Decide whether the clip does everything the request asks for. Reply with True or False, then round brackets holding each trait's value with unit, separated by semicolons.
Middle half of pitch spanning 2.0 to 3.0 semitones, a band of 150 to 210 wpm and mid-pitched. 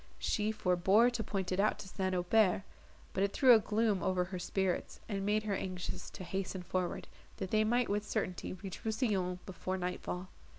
False (2.7 semitones; 195 wpm; 195 Hz)